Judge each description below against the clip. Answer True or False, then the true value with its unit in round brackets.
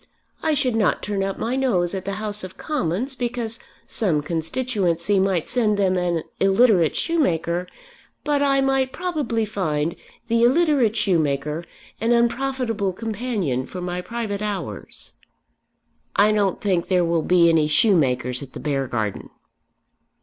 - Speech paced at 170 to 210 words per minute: False (140 wpm)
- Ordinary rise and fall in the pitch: False (5.9 semitones)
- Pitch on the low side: False (200 Hz)